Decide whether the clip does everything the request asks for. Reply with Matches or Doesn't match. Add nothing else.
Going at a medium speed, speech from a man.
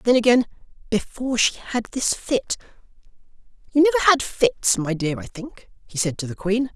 Matches